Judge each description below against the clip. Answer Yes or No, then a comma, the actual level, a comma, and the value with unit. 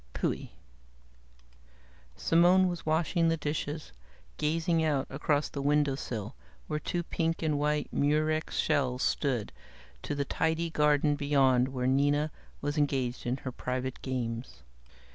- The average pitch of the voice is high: No, medium, 145 Hz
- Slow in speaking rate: Yes, slow, 125 wpm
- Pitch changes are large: No, average, 2.9 semitones